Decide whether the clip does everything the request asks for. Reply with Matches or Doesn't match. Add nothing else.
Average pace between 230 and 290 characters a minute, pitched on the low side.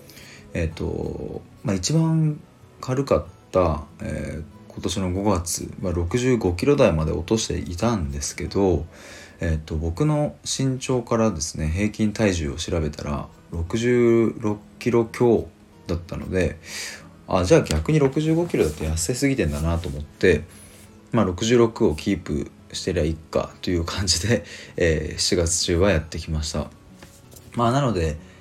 Matches